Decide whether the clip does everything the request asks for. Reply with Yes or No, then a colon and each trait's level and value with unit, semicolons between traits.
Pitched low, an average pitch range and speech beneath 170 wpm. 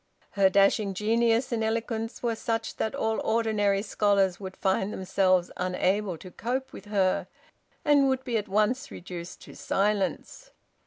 No: high, 210 Hz; average, 3.0 semitones; average, 150 wpm